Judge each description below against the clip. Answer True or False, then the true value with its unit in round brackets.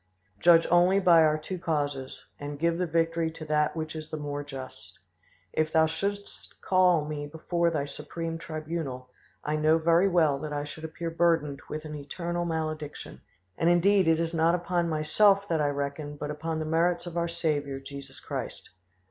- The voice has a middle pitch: True (160 Hz)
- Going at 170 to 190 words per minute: True (180 wpm)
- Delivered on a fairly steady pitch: True (2.2 semitones)